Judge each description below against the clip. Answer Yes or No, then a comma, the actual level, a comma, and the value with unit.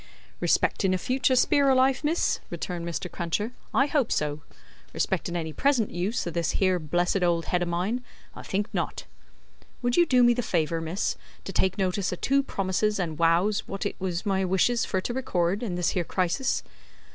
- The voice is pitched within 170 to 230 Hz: Yes, high, 190 Hz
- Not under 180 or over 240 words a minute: Yes, average, 190 wpm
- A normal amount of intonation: No, wide, 5.7 semitones